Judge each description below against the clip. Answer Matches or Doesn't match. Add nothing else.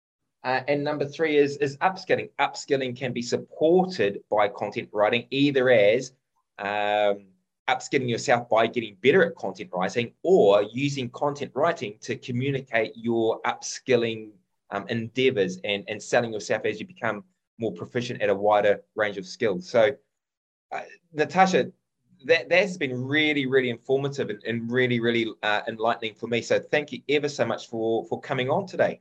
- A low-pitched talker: Matches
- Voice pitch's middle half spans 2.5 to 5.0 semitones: Matches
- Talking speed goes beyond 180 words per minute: Doesn't match